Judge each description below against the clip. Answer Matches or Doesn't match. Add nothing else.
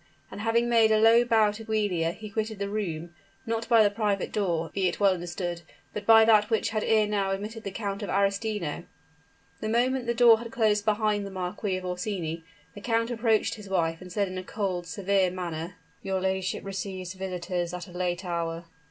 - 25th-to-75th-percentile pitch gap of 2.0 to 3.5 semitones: Matches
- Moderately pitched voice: Doesn't match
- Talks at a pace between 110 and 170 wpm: Doesn't match